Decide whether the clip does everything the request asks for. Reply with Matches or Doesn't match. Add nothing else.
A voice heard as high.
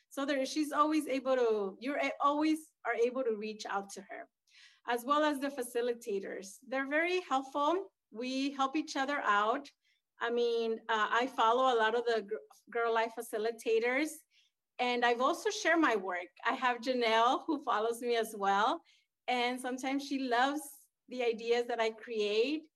Matches